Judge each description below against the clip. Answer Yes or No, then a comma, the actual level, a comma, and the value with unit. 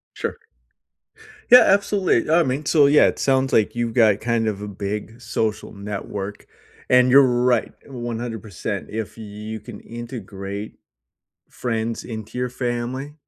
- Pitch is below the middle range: Yes, low, 115 Hz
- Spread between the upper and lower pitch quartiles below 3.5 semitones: Yes, average, 3.0 semitones